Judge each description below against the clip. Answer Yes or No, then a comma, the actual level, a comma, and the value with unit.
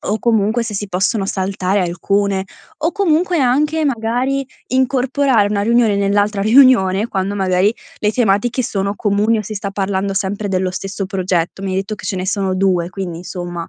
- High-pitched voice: Yes, high, 200 Hz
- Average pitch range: Yes, average, 3.5 semitones